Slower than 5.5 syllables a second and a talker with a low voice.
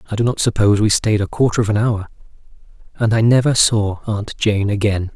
No: 5.7 syllables/s; low, 110 Hz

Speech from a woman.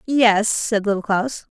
Yes: female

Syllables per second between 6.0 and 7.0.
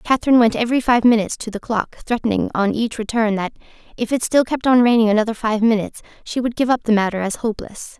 Yes: 6.6 syllables/s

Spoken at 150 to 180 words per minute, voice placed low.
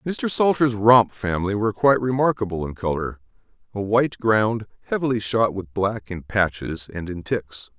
Yes: average, 155 wpm; low, 105 Hz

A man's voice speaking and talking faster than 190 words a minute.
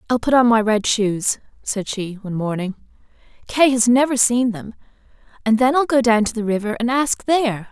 No: female; average, 200 wpm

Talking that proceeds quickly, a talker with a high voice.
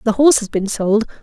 Yes: fast, 245 wpm; high, 225 Hz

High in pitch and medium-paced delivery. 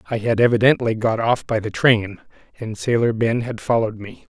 No: low, 115 Hz; average, 195 wpm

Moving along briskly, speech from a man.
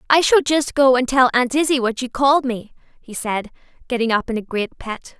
No: fast, 230 wpm; female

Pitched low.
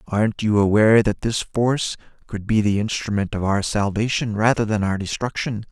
Yes: low, 105 Hz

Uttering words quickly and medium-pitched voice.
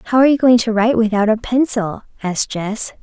No: fast, 220 wpm; high, 225 Hz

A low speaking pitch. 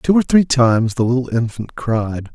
Yes: low, 125 Hz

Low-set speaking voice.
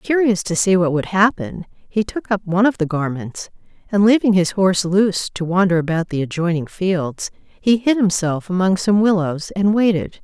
No: medium, 185 Hz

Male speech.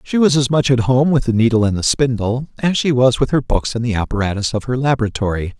Yes: male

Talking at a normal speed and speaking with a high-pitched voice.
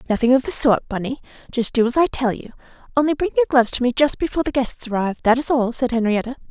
No: fast, 240 wpm; very high, 255 Hz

